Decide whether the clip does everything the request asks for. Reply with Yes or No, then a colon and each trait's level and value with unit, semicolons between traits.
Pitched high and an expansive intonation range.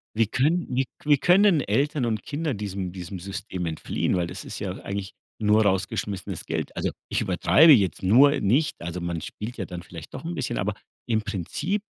No: low, 105 Hz; wide, 7.2 semitones